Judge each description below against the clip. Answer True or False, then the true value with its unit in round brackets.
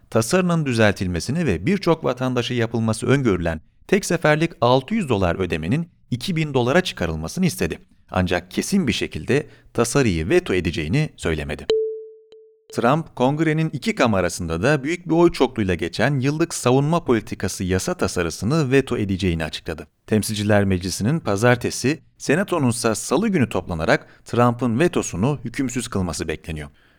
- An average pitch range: False (8.5 semitones)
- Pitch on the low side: True (125 Hz)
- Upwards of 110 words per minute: True (120 wpm)